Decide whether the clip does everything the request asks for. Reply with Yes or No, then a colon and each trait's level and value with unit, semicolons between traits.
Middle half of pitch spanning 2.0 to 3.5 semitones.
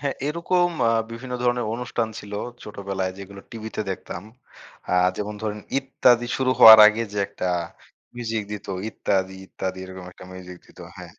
No: average, 4.2 semitones